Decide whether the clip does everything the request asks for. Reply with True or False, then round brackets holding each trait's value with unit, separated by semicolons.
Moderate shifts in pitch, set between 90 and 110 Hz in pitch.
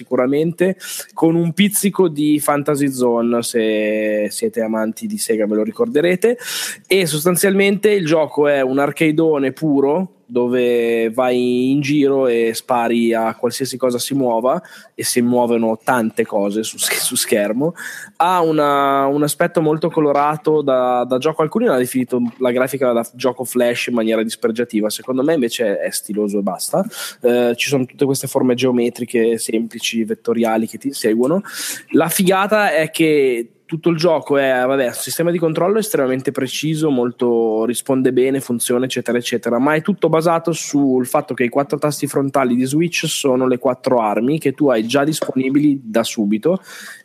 False (4.6 semitones; 130 Hz)